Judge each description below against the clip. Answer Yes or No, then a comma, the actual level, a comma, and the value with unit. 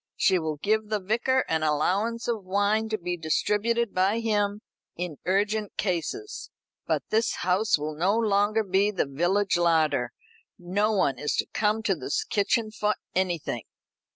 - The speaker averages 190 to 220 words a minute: No, average, 155 wpm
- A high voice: Yes, high, 200 Hz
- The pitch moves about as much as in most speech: Yes, average, 3.8 semitones